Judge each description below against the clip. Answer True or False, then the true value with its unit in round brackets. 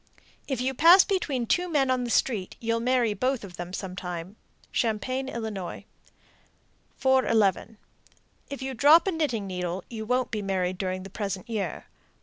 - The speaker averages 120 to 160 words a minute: True (155 wpm)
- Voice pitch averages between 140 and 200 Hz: False (230 Hz)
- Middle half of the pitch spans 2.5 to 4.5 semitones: False (5.5 semitones)